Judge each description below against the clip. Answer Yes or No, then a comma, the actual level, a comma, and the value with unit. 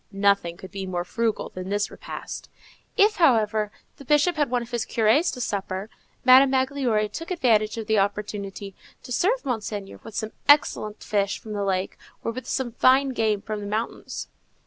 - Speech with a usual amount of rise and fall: Yes, average, 4.1 semitones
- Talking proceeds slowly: No, average, 180 wpm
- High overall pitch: Yes, high, 220 Hz